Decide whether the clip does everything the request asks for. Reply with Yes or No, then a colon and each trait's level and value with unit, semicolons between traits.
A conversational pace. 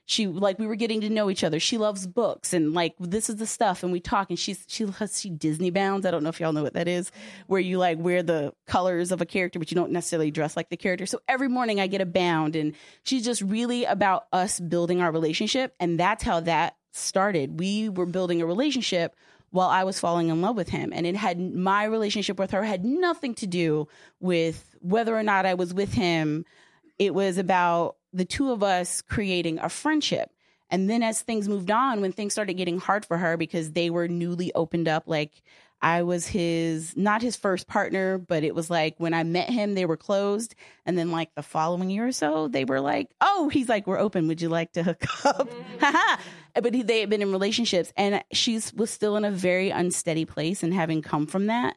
No: fast, 230 wpm